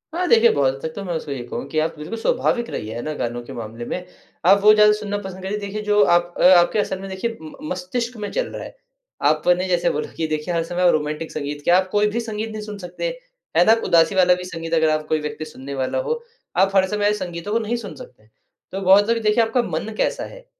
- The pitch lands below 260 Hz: Yes, medium, 185 Hz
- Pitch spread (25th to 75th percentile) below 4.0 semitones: No, average, 5.2 semitones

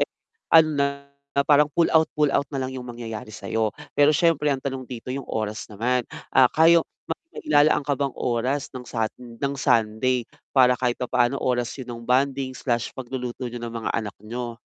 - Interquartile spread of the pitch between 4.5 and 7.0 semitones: No, average, 2.8 semitones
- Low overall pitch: Yes, low, 130 Hz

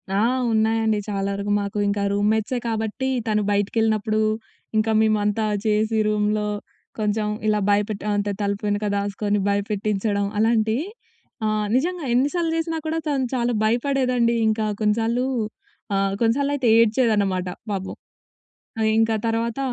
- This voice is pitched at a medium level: No, high, 215 Hz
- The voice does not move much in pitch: Yes, narrow, 2.1 semitones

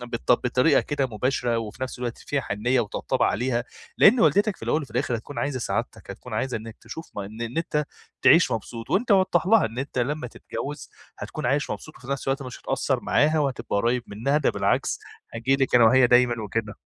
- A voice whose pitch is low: Yes, low, 125 Hz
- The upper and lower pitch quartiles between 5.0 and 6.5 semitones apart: No, average, 3.6 semitones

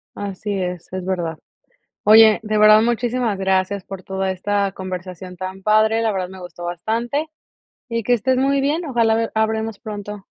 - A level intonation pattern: No, average, 3.1 semitones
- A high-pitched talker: Yes, high, 205 Hz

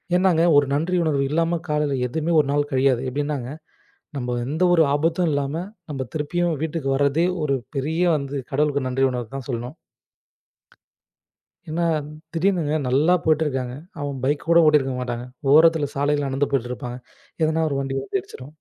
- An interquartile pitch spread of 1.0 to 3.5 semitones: Yes, average, 3.0 semitones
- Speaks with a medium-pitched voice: Yes, medium, 145 Hz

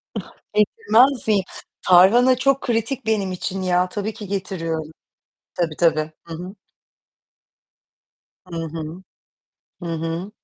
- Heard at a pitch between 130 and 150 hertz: No, medium, 185 Hz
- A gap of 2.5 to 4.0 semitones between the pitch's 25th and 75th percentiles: No, average, 4.8 semitones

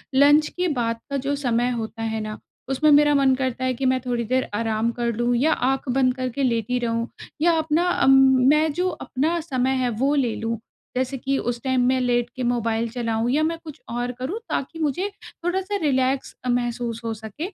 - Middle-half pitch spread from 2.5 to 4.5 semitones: Yes, average, 3.4 semitones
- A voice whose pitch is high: Yes, very high, 255 Hz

